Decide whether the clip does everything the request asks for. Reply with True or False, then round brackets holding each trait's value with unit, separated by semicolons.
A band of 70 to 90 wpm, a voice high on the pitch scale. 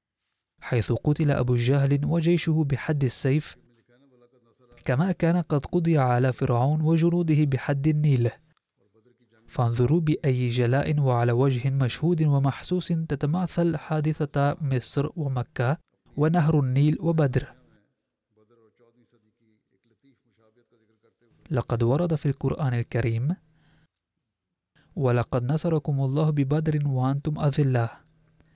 False (85 wpm; 135 Hz)